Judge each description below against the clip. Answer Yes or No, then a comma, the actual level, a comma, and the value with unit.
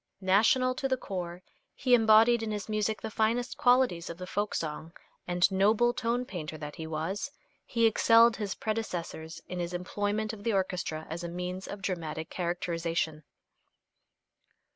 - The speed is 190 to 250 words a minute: No, average, 160 wpm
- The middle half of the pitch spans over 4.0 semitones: Yes, average, 4.7 semitones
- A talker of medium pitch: No, high, 195 Hz